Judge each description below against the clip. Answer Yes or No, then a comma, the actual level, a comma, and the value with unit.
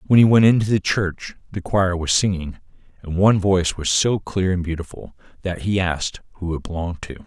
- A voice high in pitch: No, very low, 90 Hz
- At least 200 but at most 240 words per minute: Yes, fast, 205 wpm